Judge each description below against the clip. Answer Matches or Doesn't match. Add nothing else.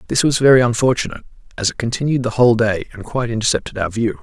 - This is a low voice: Matches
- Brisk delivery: Matches